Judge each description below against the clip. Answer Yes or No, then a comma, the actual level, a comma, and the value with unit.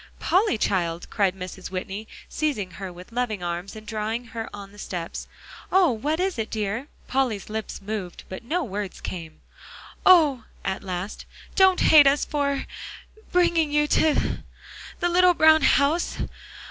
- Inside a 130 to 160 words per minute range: Yes, average, 150 wpm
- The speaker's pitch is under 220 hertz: No, high, 225 Hz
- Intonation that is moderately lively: No, wide, 7.7 semitones